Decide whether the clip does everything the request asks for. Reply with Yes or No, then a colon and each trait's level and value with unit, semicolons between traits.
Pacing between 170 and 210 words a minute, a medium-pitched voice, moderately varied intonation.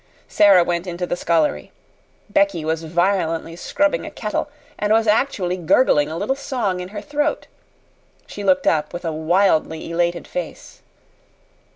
No: average, 150 wpm; medium, 180 Hz; average, 4.1 semitones